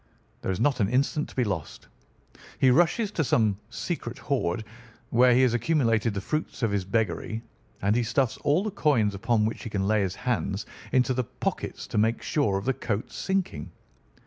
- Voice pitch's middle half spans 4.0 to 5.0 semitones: Yes, average, 4.6 semitones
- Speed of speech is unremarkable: Yes, average, 195 wpm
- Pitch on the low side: Yes, low, 115 Hz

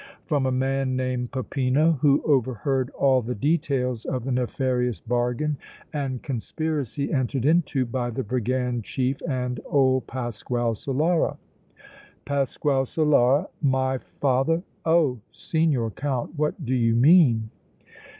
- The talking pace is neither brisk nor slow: No, slow, 120 wpm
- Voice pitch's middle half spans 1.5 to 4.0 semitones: Yes, narrow, 2.6 semitones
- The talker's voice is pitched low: Yes, low, 130 Hz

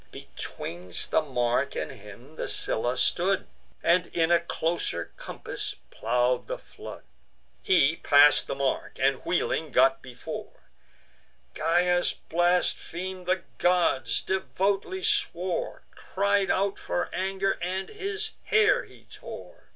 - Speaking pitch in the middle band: Yes, medium, 175 Hz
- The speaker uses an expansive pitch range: Yes, wide, 6.0 semitones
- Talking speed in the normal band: No, slow, 120 wpm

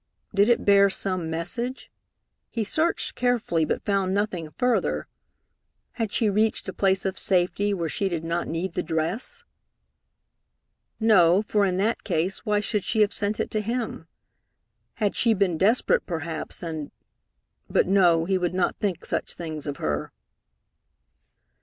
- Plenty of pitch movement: No, average, 4.0 semitones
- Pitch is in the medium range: No, high, 195 Hz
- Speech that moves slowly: No, average, 155 wpm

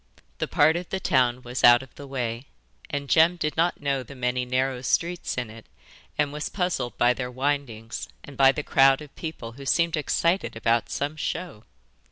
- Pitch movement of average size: Yes, average, 3.6 semitones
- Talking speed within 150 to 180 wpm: No, average, 195 wpm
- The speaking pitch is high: No, low, 135 Hz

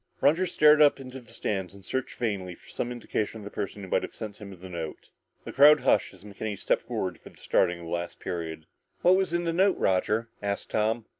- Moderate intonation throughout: No, wide, 6.1 semitones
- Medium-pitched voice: No, low, 105 Hz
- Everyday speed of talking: No, fast, 235 wpm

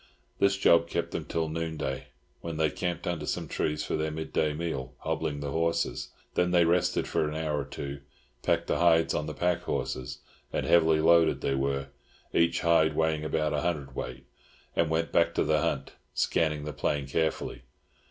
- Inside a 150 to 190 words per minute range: Yes, average, 180 wpm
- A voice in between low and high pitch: No, very low, 80 Hz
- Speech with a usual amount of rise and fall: No, narrow, 2.1 semitones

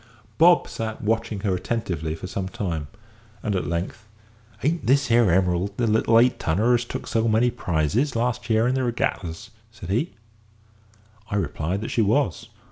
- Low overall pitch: Yes, low, 110 Hz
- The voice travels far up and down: No, average, 4.3 semitones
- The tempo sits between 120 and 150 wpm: No, average, 170 wpm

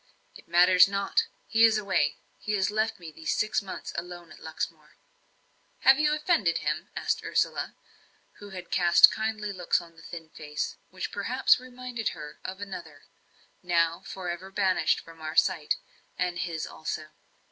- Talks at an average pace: Yes, average, 160 wpm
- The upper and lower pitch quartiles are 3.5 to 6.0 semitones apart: Yes, average, 4.2 semitones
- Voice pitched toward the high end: No, medium, 180 Hz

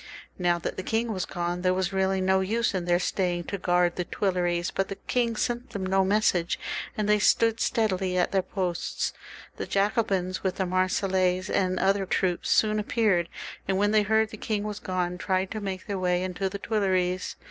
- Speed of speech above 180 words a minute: Yes, average, 200 wpm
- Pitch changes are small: Yes, narrow, 2.3 semitones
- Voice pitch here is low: No, high, 190 Hz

